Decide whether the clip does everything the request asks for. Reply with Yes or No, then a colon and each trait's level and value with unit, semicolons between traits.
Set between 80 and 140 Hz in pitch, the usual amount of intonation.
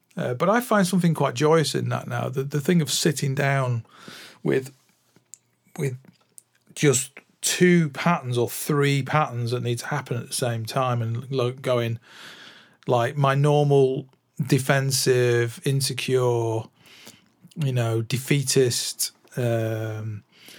Yes: low, 135 Hz; average, 3.4 semitones